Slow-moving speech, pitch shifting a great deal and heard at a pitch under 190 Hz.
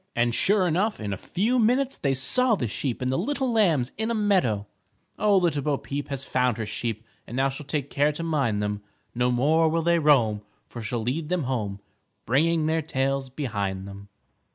No: average, 200 wpm; wide, 6.1 semitones; medium, 140 Hz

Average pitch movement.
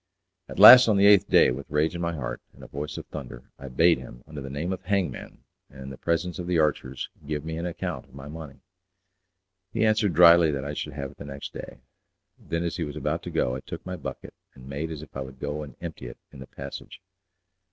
Yes: average, 4.0 semitones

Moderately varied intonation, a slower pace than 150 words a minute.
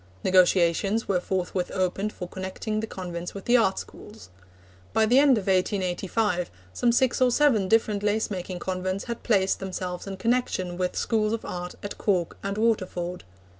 No: average, 3.3 semitones; average, 170 wpm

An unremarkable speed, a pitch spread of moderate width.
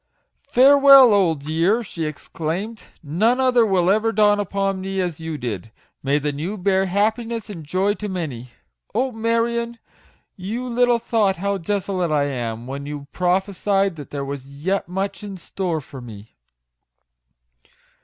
No: average, 155 wpm; wide, 6.0 semitones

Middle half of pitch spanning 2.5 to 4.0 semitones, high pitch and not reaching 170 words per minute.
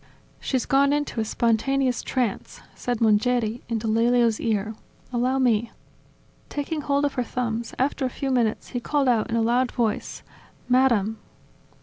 Yes: average, 2.8 semitones; high, 245 Hz; average, 150 wpm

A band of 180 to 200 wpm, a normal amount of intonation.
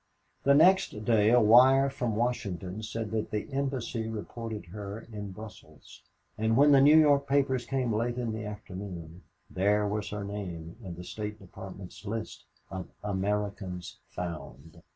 No: average, 150 wpm; average, 3.7 semitones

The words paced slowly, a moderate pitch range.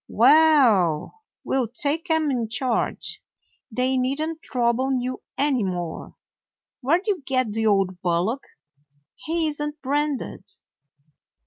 Yes: slow, 125 wpm; average, 5.0 semitones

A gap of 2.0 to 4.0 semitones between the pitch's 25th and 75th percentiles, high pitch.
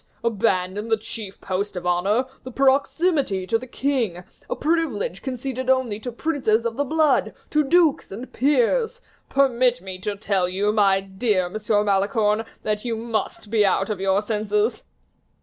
No: average, 4.7 semitones; high, 220 Hz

